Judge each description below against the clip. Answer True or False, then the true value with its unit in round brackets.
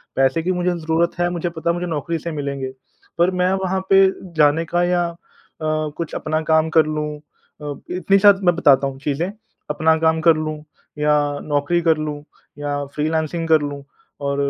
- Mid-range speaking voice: True (160 Hz)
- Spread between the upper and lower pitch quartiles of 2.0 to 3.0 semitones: True (2.6 semitones)